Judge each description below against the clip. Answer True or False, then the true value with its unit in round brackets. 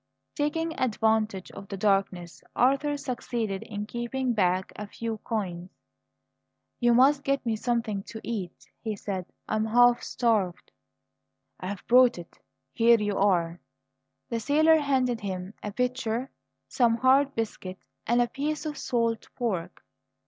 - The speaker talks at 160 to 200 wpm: False (140 wpm)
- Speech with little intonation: False (4.1 semitones)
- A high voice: True (230 Hz)